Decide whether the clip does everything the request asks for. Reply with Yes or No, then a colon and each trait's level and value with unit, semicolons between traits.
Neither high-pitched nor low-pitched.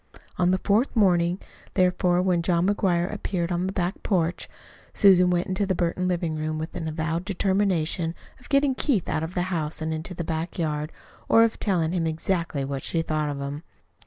Yes: medium, 175 Hz